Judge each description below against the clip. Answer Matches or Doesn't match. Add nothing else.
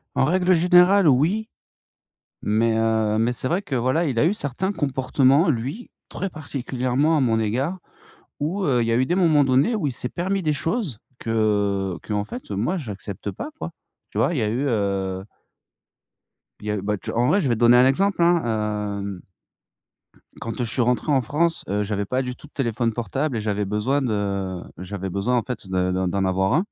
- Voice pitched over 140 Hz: Doesn't match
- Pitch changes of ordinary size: Doesn't match